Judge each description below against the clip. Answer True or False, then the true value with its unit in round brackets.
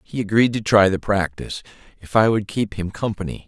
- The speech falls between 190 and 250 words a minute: True (205 wpm)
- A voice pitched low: True (105 Hz)